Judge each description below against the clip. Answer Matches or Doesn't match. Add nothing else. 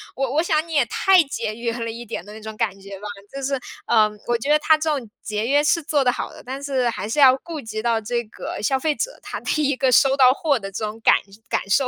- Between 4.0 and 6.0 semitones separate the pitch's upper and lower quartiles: Matches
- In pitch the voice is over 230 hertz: Matches